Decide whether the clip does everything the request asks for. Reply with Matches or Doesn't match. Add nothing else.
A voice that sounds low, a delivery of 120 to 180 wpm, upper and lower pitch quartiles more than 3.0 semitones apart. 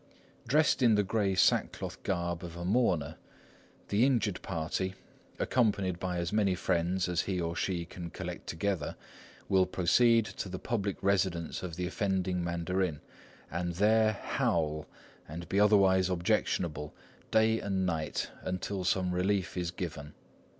Doesn't match